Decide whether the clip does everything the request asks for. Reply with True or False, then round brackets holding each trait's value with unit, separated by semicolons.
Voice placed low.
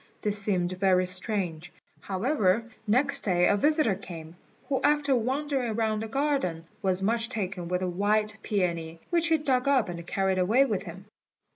False (205 Hz)